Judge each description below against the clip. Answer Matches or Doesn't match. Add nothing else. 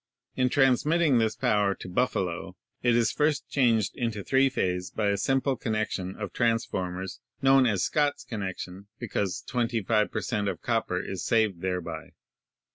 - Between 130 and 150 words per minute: Doesn't match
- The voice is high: Doesn't match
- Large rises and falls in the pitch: Doesn't match